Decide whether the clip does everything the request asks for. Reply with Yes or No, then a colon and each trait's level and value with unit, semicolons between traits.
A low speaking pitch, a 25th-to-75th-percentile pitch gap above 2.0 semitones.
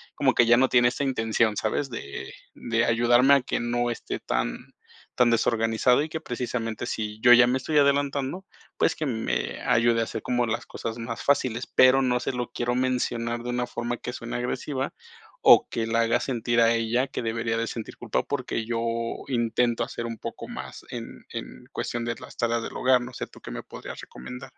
No: low, 120 Hz; narrow, 1.7 semitones